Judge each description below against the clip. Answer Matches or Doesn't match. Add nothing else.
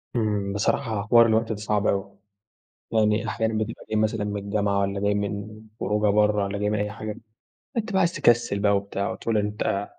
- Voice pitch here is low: Matches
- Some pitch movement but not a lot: Doesn't match